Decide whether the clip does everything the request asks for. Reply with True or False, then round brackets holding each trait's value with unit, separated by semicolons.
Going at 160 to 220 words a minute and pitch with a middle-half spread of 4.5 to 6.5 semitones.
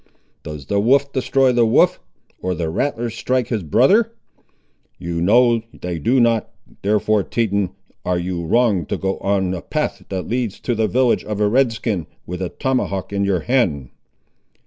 True (170 wpm; 5.0 semitones)